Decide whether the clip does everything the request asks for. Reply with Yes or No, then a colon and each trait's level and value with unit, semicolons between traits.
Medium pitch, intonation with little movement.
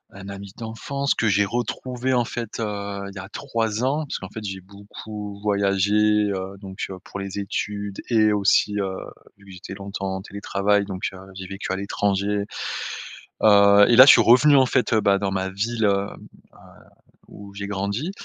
No: low, 100 Hz; narrow, 2.0 semitones